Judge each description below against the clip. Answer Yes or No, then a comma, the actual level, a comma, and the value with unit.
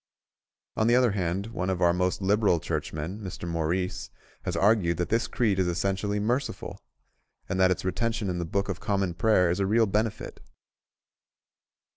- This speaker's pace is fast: No, average, 170 wpm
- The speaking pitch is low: Yes, very low, 95 Hz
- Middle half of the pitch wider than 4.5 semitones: No, average, 3.2 semitones